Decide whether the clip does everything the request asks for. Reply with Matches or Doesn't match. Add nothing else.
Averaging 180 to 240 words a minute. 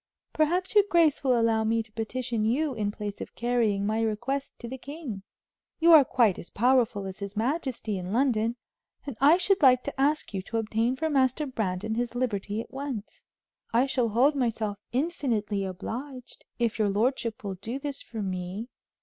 Matches